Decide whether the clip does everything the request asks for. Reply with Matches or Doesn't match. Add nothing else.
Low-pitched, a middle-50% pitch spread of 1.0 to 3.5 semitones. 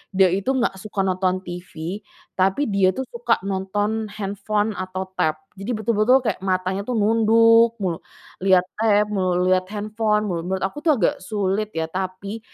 Doesn't match